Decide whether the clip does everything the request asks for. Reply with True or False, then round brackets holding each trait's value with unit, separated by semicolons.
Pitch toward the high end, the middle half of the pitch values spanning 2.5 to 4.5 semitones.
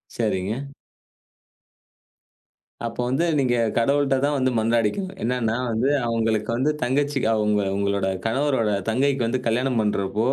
False (115 Hz; 3.5 semitones)